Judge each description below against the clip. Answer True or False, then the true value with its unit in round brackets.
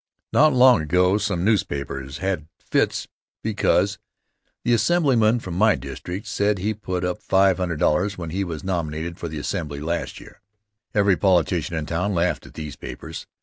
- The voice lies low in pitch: True (90 Hz)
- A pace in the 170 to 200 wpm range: False (160 wpm)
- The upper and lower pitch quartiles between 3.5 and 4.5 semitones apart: True (4.1 semitones)